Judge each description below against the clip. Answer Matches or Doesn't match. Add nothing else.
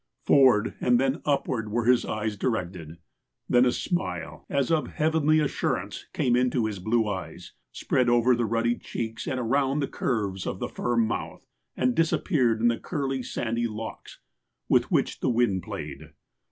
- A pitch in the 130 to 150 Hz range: Doesn't match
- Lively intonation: Doesn't match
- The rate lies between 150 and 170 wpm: Matches